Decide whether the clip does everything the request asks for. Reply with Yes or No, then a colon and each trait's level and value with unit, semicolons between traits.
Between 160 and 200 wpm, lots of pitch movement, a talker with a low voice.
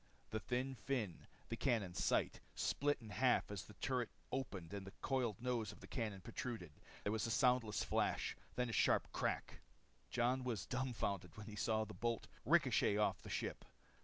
No: average, 180 wpm; average, 3.4 semitones; low, 115 Hz